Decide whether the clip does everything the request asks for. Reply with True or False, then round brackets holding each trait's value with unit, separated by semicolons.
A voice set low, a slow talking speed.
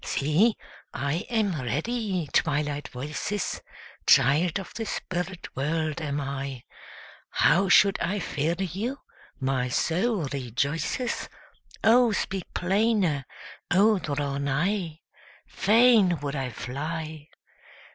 False (165 Hz; 105 wpm)